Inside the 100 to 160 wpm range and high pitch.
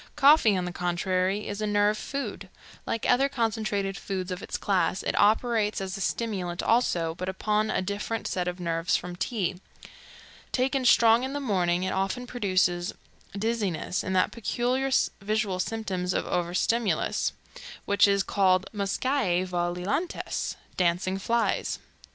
Yes: average, 145 wpm; high, 200 Hz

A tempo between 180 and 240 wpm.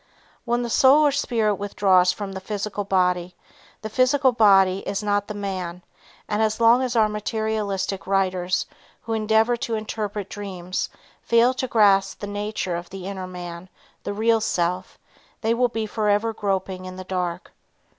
No: average, 165 wpm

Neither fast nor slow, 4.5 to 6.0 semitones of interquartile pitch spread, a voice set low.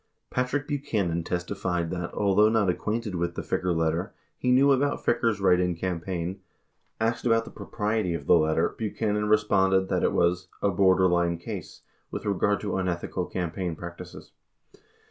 No: average, 160 wpm; average, 3.6 semitones; very low, 95 Hz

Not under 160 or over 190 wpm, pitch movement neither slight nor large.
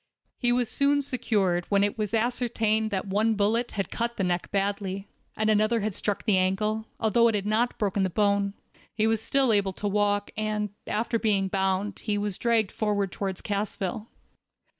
No: average, 185 wpm; narrow, 2.0 semitones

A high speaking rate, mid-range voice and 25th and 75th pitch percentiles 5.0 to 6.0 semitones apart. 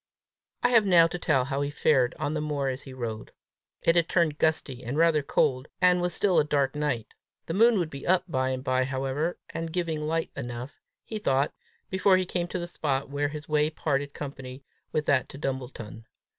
No: fast, 210 wpm; medium, 150 Hz; average, 3.9 semitones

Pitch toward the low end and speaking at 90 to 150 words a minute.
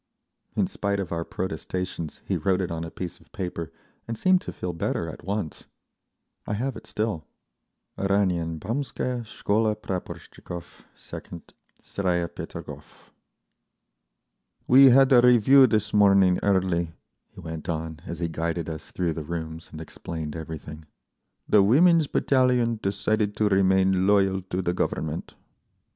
Yes: very low, 95 Hz; average, 140 wpm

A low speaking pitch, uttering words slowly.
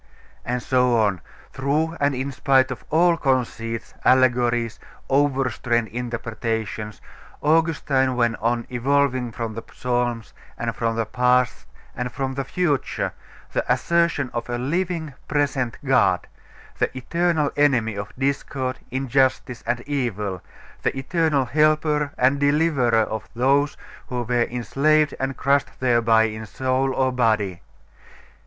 Yes: low, 130 Hz; slow, 125 wpm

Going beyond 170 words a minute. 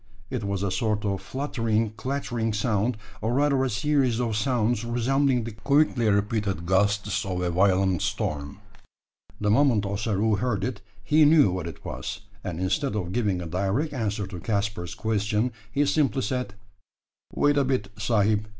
No: average, 160 wpm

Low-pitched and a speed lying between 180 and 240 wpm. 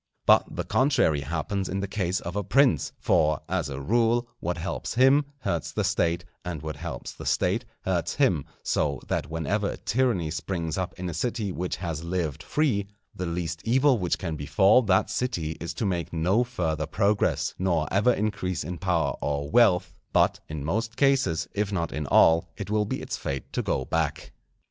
Yes: very low, 90 Hz; average, 190 wpm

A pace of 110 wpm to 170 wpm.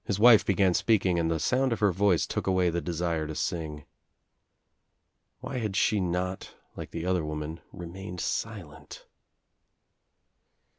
Yes: average, 150 wpm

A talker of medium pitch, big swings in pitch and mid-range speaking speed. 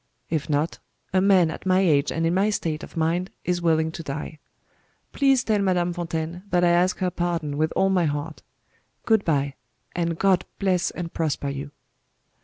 No: medium, 170 Hz; average, 2.7 semitones; average, 185 wpm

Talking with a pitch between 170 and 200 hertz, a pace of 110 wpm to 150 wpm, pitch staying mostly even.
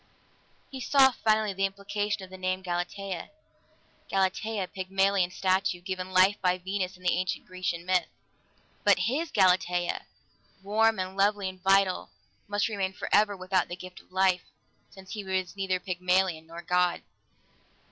Yes: high, 190 Hz; average, 145 wpm; narrow, 1.5 semitones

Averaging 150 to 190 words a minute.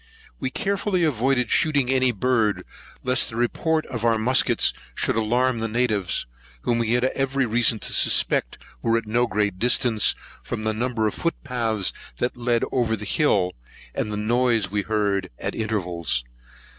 Yes: average, 170 wpm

